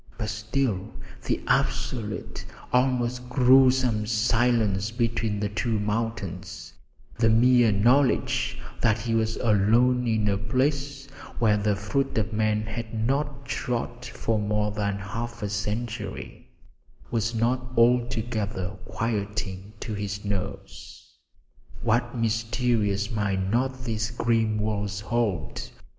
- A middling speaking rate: No, slow, 115 wpm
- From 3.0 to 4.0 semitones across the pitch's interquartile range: No, narrow, 2.6 semitones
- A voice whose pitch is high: No, low, 110 Hz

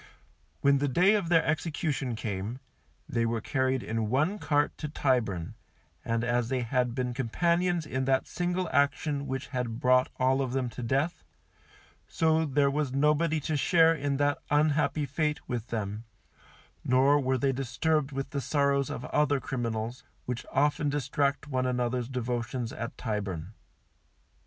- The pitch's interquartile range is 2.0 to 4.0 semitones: Yes, average, 3.3 semitones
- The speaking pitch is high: No, low, 135 Hz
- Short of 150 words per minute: No, average, 155 wpm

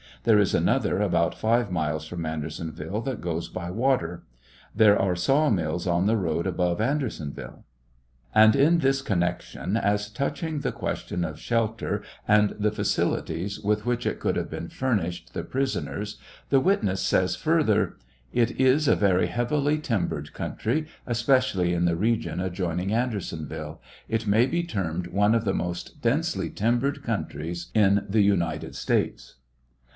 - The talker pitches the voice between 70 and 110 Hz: Yes, low, 105 Hz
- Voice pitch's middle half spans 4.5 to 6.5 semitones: Yes, wide, 5.5 semitones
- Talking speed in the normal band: Yes, average, 150 wpm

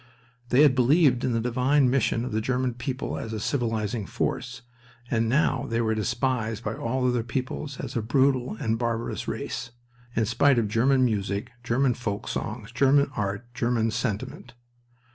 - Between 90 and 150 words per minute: No, average, 165 wpm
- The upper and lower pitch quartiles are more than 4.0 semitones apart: No, narrow, 2.4 semitones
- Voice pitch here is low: Yes, low, 120 Hz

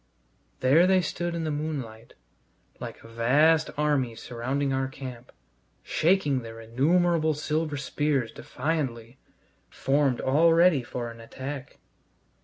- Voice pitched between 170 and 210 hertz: No, medium, 140 Hz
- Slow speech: Yes, slow, 120 wpm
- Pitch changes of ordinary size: Yes, average, 4.3 semitones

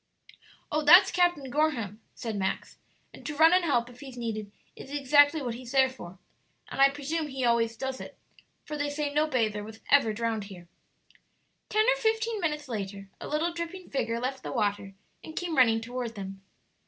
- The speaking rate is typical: Yes, average, 190 wpm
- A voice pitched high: Yes, very high, 265 Hz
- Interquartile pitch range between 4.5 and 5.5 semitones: Yes, average, 5.1 semitones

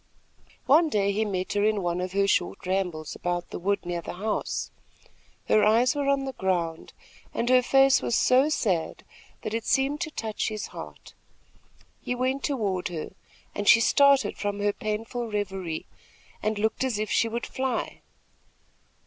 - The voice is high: Yes, high, 215 Hz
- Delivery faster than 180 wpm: No, average, 170 wpm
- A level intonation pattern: No, average, 5.0 semitones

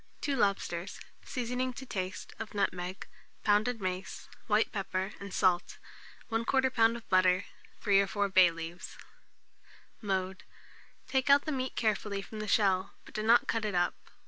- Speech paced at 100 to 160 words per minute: Yes, average, 155 wpm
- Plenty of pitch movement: No, average, 3.6 semitones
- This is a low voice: No, high, 205 Hz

